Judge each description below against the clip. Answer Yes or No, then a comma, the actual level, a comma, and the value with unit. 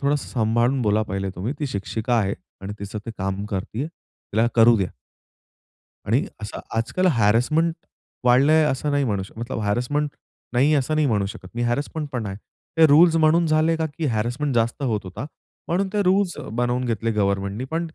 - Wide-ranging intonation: Yes, wide, 6.0 semitones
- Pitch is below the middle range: Yes, low, 120 Hz